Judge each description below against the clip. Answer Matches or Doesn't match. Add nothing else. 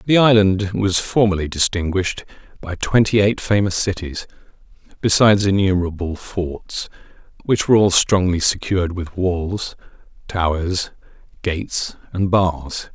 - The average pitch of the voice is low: Matches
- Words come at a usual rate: Doesn't match